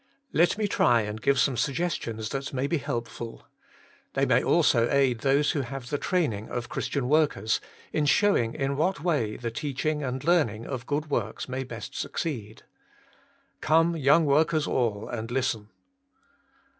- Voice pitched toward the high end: No, low, 135 Hz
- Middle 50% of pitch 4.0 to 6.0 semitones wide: Yes, average, 4.4 semitones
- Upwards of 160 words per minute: No, average, 155 wpm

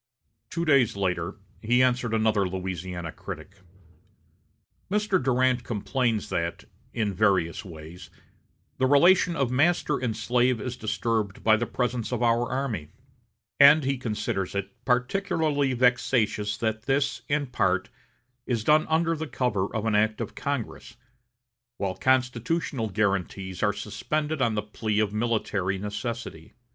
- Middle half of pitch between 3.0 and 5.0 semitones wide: Yes, average, 4.3 semitones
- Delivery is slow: Yes, slow, 130 wpm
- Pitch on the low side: Yes, low, 115 Hz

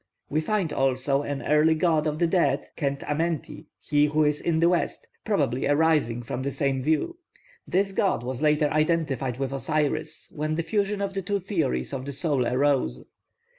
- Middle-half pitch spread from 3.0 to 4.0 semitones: Yes, average, 3.3 semitones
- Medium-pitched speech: Yes, medium, 150 Hz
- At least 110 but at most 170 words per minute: No, average, 180 wpm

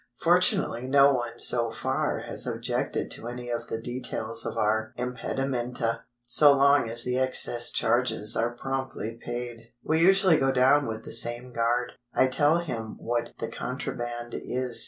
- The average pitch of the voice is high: No, low, 120 Hz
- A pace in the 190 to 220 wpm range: No, average, 155 wpm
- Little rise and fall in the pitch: Yes, narrow, 2.1 semitones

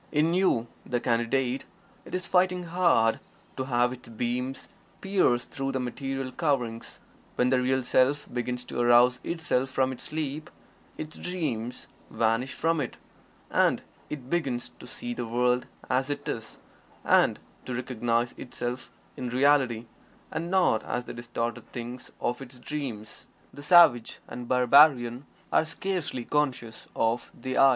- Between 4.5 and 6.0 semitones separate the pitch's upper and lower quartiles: No, average, 3.5 semitones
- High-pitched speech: No, low, 130 Hz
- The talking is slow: No, average, 145 wpm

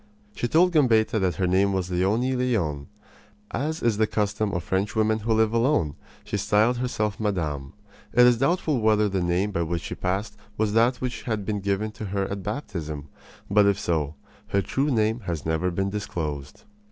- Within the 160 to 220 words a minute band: Yes, average, 185 wpm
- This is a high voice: No, low, 105 Hz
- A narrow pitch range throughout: No, average, 3.9 semitones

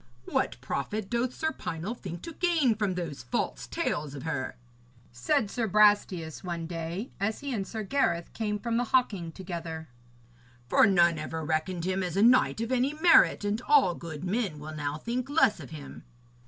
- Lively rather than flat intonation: Yes, wide, 6.3 semitones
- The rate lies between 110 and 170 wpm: No, average, 180 wpm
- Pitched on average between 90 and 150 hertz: No, high, 190 Hz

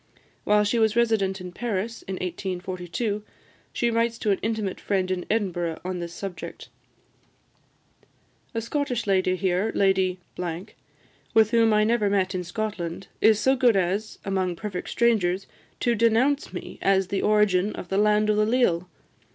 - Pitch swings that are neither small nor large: Yes, average, 3.2 semitones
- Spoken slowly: No, average, 155 wpm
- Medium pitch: No, high, 205 Hz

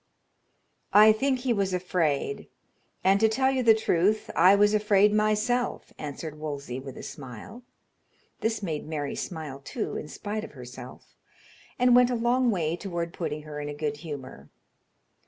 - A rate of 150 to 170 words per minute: Yes, average, 160 wpm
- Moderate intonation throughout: No, wide, 6.5 semitones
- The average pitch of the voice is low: No, medium, 185 Hz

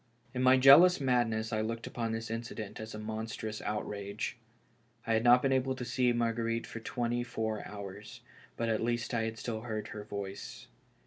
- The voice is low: Yes, low, 115 Hz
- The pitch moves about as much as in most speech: No, narrow, 1.9 semitones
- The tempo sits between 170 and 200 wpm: Yes, average, 190 wpm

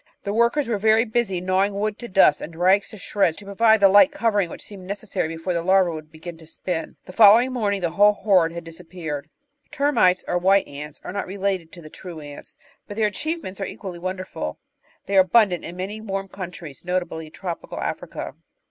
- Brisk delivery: Yes, fast, 210 wpm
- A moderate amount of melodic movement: Yes, average, 3.3 semitones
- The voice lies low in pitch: No, high, 190 Hz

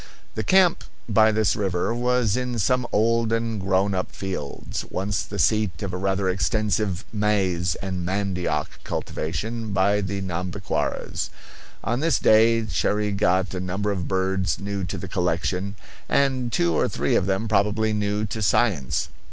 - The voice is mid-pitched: No, low, 100 Hz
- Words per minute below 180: Yes, average, 155 wpm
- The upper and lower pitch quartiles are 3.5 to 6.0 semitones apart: No, average, 2.8 semitones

